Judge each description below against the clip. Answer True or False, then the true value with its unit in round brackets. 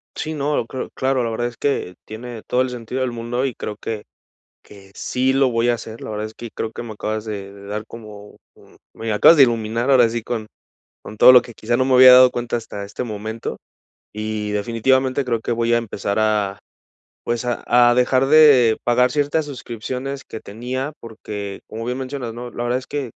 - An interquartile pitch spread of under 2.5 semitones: False (2.8 semitones)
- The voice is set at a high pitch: False (120 Hz)